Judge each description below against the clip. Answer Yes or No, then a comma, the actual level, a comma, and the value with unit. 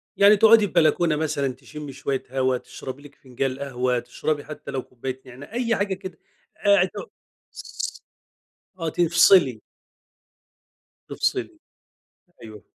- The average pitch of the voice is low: No, medium, 145 Hz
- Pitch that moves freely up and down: Yes, wide, 6.3 semitones